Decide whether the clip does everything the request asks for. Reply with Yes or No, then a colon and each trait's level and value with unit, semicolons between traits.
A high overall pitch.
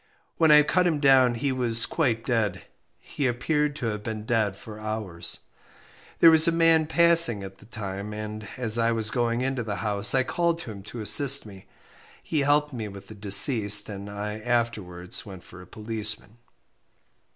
No: low, 115 Hz